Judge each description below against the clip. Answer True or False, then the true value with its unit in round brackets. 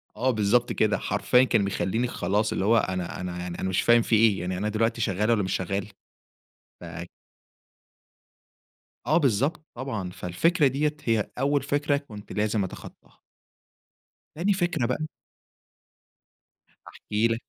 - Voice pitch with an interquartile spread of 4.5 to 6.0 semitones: True (5.3 semitones)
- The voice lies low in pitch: True (115 Hz)